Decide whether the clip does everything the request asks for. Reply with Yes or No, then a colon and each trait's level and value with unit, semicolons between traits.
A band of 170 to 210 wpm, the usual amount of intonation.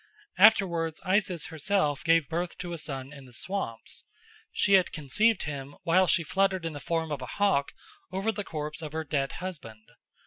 Yes: average, 180 wpm; average, 4.5 semitones